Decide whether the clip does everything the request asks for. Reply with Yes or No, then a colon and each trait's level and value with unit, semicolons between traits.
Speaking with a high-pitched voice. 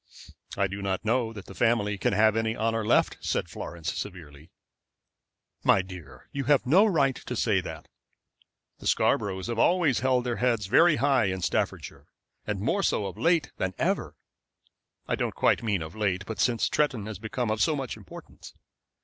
No: low, 110 Hz